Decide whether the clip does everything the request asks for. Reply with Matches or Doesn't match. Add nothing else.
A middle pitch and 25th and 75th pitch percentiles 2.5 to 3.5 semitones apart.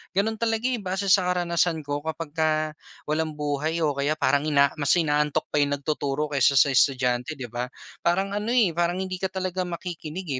Doesn't match